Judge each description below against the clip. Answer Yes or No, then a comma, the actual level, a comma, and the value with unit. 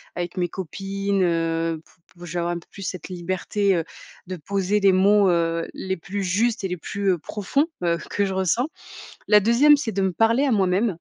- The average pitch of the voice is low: No, high, 190 Hz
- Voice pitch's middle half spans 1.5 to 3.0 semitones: Yes, average, 2.7 semitones